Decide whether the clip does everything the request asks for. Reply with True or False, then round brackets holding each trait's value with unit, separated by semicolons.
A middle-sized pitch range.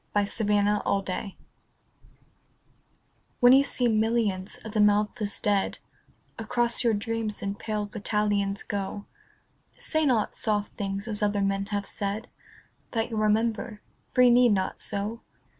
False (2.0 semitones)